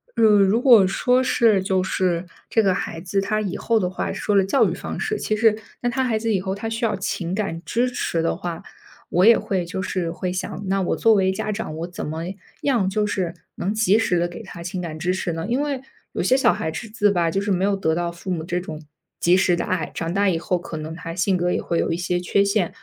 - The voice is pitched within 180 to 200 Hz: Yes, high, 190 Hz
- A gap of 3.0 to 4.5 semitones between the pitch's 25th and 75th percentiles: Yes, average, 3.6 semitones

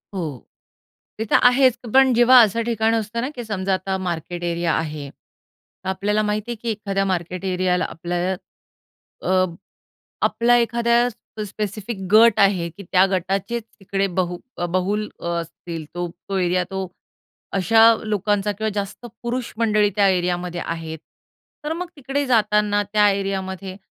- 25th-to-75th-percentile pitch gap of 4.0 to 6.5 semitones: No, average, 3.6 semitones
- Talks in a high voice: Yes, high, 200 Hz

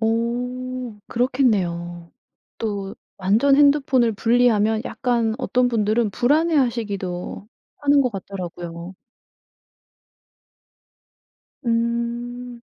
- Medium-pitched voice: No, high, 235 Hz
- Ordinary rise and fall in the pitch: Yes, average, 3.5 semitones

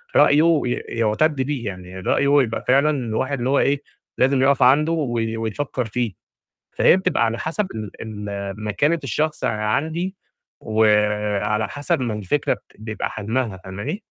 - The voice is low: Yes, low, 120 Hz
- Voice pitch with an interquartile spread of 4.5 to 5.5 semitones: Yes, average, 5.2 semitones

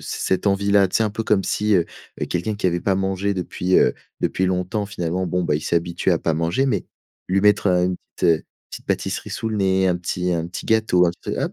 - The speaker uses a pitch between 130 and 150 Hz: No, very low, 95 Hz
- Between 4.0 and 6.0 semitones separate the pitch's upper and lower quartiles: No, narrow, 2.4 semitones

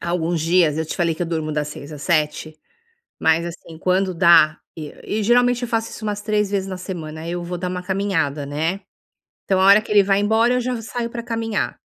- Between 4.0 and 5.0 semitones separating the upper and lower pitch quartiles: Yes, average, 4.5 semitones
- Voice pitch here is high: No, medium, 180 Hz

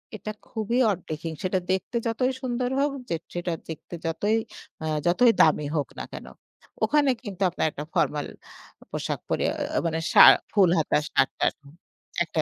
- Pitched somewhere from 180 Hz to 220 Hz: Yes, medium, 185 Hz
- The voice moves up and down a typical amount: No, wide, 6.3 semitones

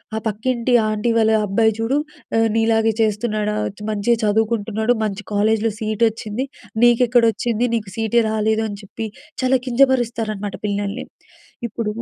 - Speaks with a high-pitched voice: Yes, high, 220 Hz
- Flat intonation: Yes, narrow, 1.8 semitones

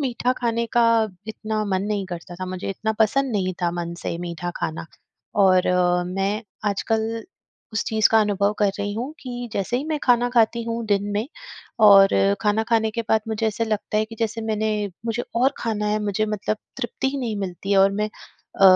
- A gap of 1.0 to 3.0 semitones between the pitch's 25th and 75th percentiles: Yes, narrow, 2.6 semitones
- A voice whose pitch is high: Yes, high, 215 Hz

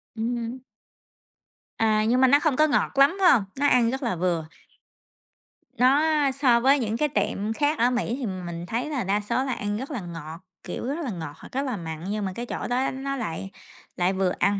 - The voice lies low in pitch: No, high, 235 Hz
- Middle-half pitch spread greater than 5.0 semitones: Yes, wide, 5.5 semitones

